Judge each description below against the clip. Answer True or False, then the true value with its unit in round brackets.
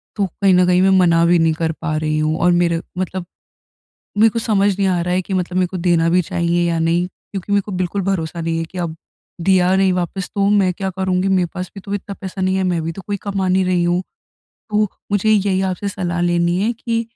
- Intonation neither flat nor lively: False (2.1 semitones)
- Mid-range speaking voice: True (180 Hz)